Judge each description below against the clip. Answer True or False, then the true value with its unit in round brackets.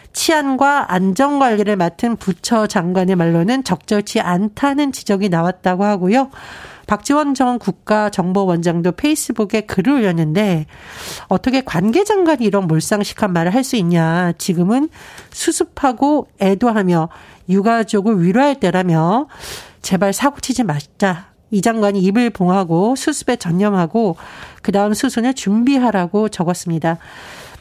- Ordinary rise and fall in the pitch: False (6.0 semitones)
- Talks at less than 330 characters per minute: True (300 characters per minute)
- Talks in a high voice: True (210 Hz)